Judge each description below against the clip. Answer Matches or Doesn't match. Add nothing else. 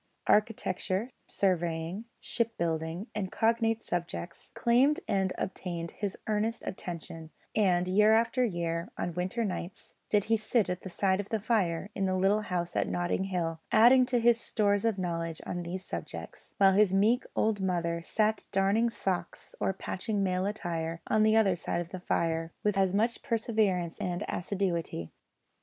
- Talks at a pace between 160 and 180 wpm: Matches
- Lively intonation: Doesn't match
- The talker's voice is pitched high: Matches